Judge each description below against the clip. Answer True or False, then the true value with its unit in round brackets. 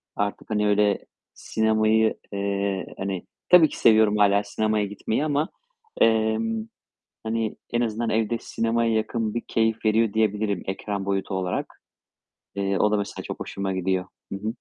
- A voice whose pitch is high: False (110 Hz)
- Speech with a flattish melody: True (2.0 semitones)